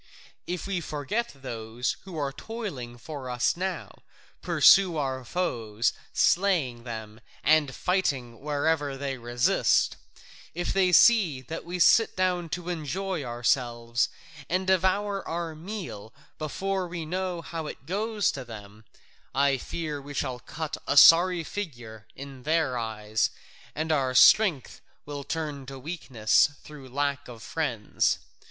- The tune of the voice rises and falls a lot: Yes, wide, 6.1 semitones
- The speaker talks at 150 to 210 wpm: No, slow, 135 wpm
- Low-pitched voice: No, medium, 145 Hz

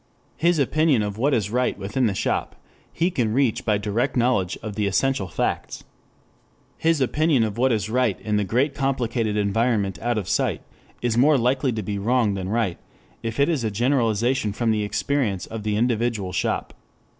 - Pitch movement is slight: No, average, 4.0 semitones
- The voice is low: Yes, low, 115 Hz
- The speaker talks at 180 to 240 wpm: Yes, average, 185 wpm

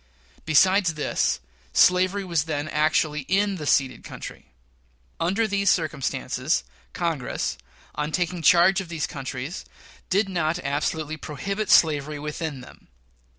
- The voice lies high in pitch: No, medium, 160 Hz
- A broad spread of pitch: No, average, 3.8 semitones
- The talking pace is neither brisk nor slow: No, slow, 120 wpm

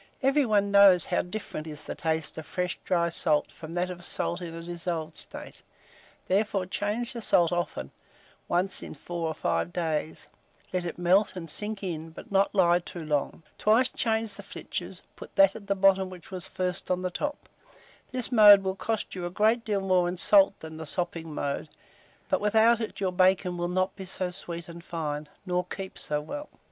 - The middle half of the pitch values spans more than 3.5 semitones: No, average, 2.9 semitones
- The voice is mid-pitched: Yes, medium, 180 Hz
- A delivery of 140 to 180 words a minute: No, average, 195 wpm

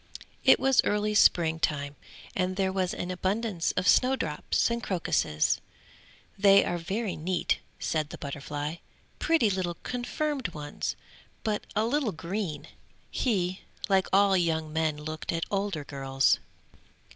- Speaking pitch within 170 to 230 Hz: Yes, medium, 185 Hz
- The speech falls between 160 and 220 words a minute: No, slow, 135 wpm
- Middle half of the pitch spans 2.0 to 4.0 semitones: No, average, 4.8 semitones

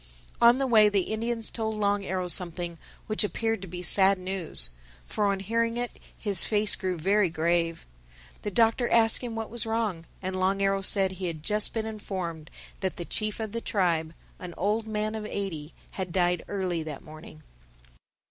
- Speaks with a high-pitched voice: Yes, high, 195 Hz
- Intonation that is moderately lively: Yes, average, 3.7 semitones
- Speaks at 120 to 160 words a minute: No, average, 185 wpm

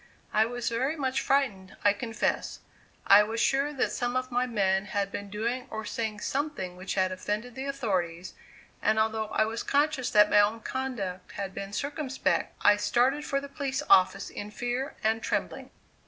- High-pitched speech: Yes, high, 225 Hz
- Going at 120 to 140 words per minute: No, average, 180 wpm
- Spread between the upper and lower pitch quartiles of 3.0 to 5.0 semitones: Yes, average, 4.4 semitones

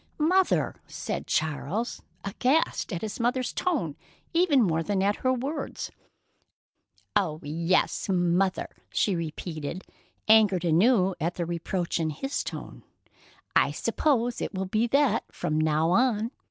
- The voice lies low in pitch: No, high, 195 Hz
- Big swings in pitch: Yes, wide, 6.6 semitones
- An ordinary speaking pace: No, slow, 130 wpm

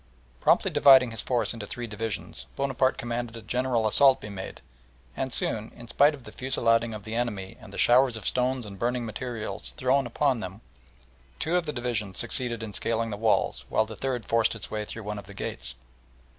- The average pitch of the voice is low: Yes, low, 115 Hz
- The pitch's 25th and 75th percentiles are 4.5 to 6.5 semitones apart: No, average, 3.0 semitones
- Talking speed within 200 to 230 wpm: Yes, fast, 205 wpm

